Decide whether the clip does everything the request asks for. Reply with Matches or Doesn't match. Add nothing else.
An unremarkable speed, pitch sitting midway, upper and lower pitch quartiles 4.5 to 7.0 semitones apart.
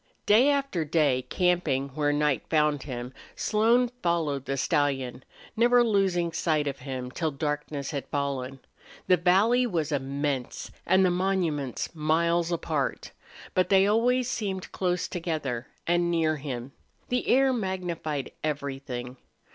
Doesn't match